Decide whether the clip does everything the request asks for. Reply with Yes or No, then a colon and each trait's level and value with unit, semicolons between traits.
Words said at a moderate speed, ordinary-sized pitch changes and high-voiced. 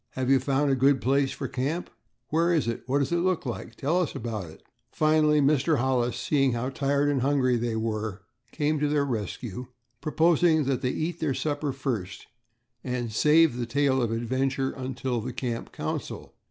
No: average, 190 wpm; average, 3.4 semitones; low, 135 Hz